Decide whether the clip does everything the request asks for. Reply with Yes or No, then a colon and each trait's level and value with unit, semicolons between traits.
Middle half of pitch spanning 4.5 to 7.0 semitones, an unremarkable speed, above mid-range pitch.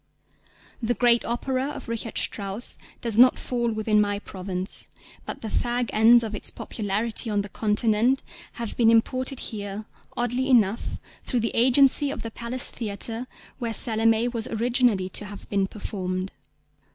No: average, 2.7 semitones; average, 150 wpm; high, 225 Hz